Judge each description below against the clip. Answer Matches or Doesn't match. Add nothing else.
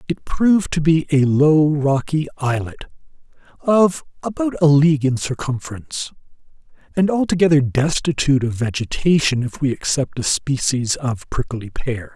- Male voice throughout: Matches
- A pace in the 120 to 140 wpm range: Matches